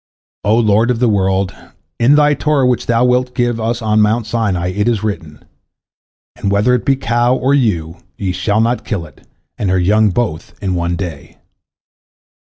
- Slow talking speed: No, average, 180 wpm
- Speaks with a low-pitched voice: Yes, low, 110 Hz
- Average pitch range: Yes, average, 4.1 semitones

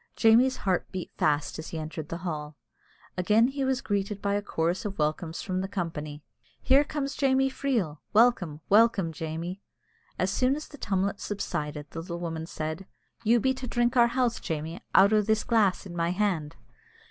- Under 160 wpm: No, average, 180 wpm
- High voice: Yes, high, 195 Hz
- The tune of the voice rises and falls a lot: Yes, wide, 6.2 semitones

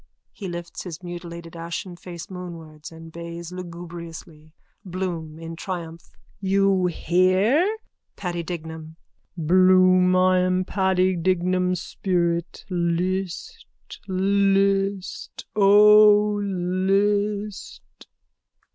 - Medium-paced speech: No, slow, 85 wpm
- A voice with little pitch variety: Yes, narrow, 2.3 semitones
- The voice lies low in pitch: No, medium, 180 Hz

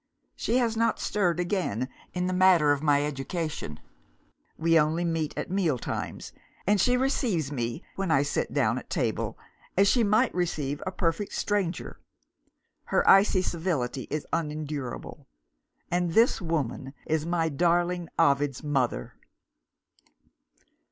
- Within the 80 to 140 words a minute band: Yes, slow, 135 wpm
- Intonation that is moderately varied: Yes, average, 4.3 semitones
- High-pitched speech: No, medium, 165 Hz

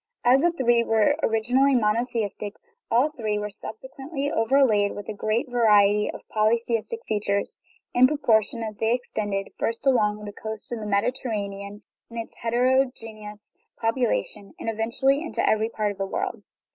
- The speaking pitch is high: Yes, high, 225 Hz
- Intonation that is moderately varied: Yes, average, 3.0 semitones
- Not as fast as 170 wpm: Yes, average, 155 wpm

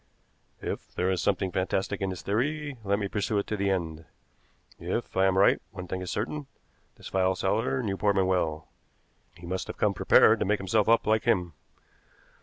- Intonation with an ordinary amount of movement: No, narrow, 2.3 semitones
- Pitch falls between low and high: No, very low, 95 Hz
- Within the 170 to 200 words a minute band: Yes, average, 195 wpm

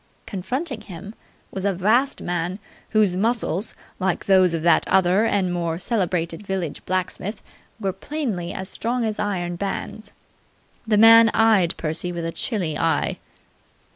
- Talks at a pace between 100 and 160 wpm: Yes, average, 140 wpm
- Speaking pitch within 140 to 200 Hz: Yes, high, 190 Hz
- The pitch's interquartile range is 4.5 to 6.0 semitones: No, average, 3.7 semitones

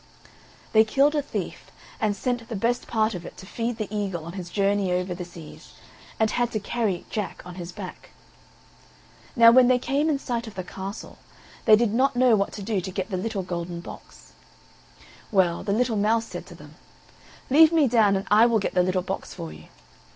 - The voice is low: No, high, 210 Hz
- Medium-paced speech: No, fast, 210 wpm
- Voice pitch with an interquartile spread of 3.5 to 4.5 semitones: Yes, average, 4.2 semitones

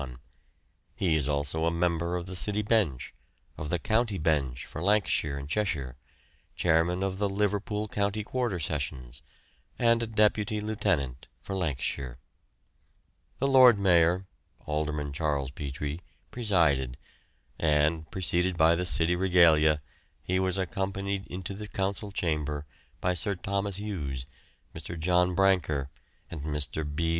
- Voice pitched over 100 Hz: No, very low, 85 Hz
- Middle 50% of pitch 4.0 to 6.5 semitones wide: Yes, average, 4.8 semitones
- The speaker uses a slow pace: Yes, slow, 130 wpm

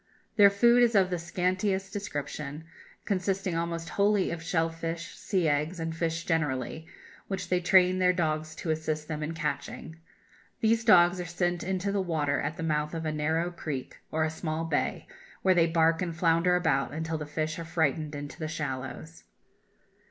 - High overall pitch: No, medium, 165 Hz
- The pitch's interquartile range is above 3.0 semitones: No, average, 2.7 semitones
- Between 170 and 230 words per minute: Yes, average, 180 wpm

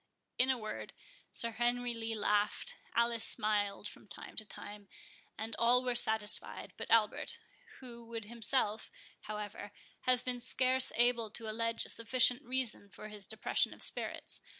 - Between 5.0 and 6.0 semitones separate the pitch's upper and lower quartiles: No, narrow, 2.4 semitones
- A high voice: Yes, high, 230 Hz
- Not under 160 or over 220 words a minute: No, average, 150 wpm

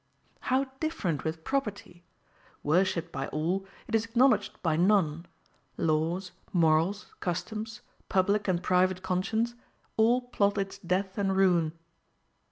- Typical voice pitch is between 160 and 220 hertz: Yes, high, 190 Hz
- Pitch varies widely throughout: No, average, 3.7 semitones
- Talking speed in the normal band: No, slow, 120 wpm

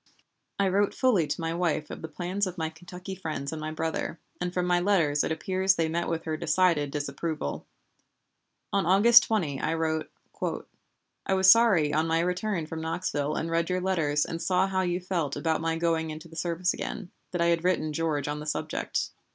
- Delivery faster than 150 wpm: Yes, average, 200 wpm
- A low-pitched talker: No, medium, 165 Hz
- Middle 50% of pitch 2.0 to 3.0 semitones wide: Yes, narrow, 2.6 semitones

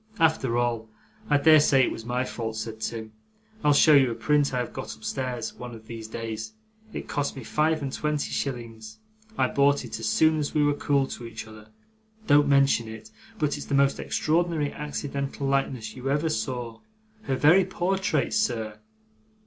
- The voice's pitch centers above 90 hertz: Yes, low, 135 Hz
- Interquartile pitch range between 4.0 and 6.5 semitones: Yes, average, 4.5 semitones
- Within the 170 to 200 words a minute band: Yes, average, 180 wpm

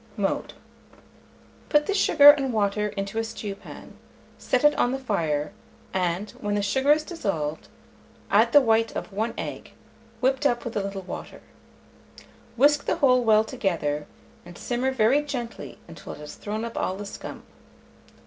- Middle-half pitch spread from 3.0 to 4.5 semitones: No, average, 5.1 semitones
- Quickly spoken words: No, average, 160 wpm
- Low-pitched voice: No, high, 225 Hz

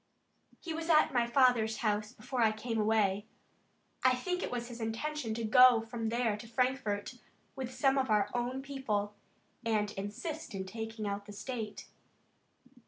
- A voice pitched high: Yes, high, 230 Hz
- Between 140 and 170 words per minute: Yes, average, 165 wpm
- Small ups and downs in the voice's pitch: No, average, 3.1 semitones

